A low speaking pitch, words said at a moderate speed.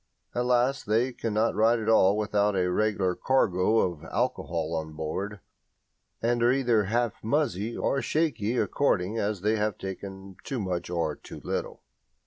Yes: low, 105 Hz; average, 155 wpm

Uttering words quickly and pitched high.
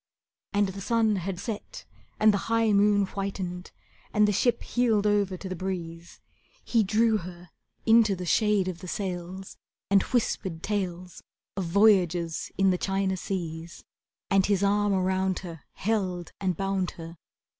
No: average, 155 wpm; high, 195 Hz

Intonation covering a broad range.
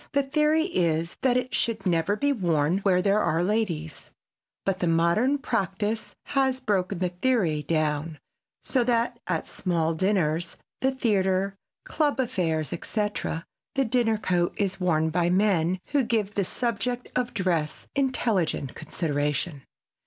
Yes: wide, 6.1 semitones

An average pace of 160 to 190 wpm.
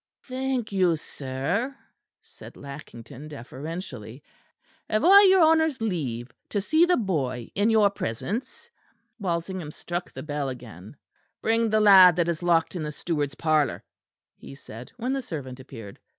No: average, 145 wpm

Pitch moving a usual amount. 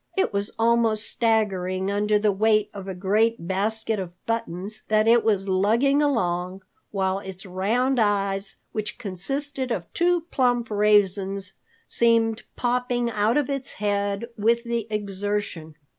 Yes: average, 3.2 semitones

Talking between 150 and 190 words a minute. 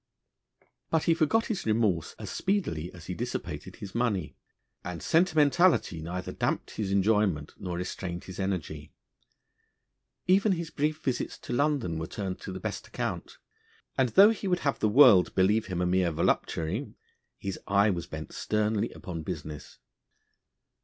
Yes: average, 155 wpm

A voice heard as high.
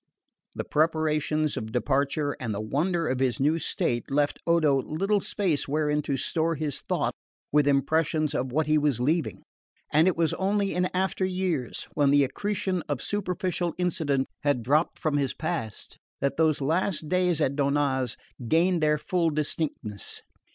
No: medium, 155 Hz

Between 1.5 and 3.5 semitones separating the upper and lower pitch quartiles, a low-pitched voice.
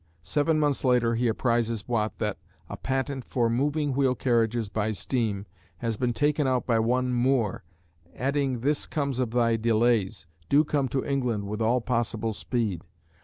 Yes: average, 2.9 semitones; low, 120 Hz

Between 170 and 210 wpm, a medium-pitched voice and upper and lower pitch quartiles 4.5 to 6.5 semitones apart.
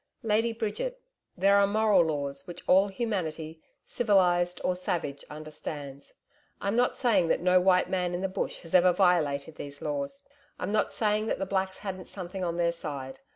No: average, 175 wpm; medium, 180 Hz; average, 4.0 semitones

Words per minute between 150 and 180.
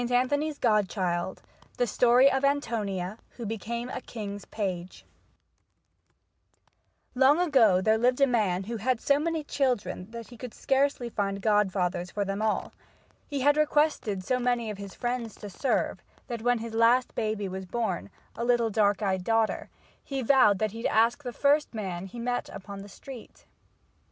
Yes: average, 165 wpm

